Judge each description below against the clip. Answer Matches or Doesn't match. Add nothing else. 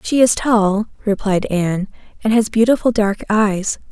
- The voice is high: Matches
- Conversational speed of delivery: Matches